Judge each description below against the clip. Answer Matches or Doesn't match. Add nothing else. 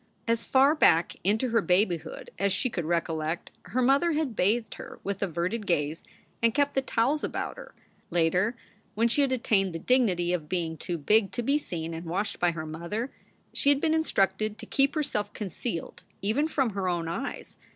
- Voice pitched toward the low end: Doesn't match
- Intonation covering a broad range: Matches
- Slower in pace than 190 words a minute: Doesn't match